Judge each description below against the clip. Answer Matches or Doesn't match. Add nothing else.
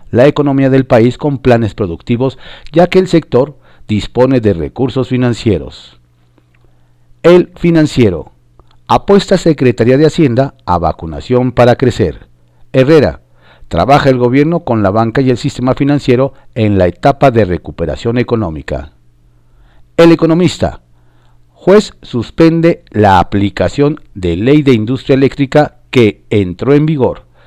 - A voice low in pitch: Matches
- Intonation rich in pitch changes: Matches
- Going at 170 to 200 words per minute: Doesn't match